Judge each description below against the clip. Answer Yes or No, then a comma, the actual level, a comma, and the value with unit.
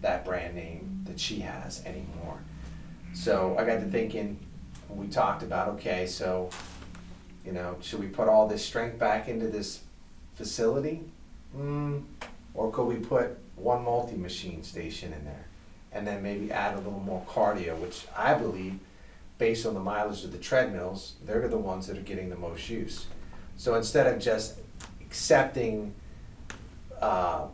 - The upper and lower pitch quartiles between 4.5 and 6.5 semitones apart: No, average, 3.3 semitones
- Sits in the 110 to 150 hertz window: No, low, 100 Hz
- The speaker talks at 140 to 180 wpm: Yes, average, 160 wpm